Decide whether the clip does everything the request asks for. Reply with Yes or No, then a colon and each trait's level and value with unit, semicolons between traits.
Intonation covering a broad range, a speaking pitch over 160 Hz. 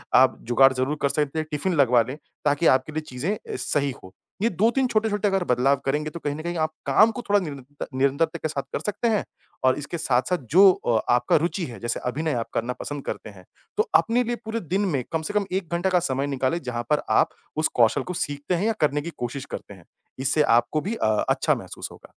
No: wide, 5.8 semitones; medium, 150 Hz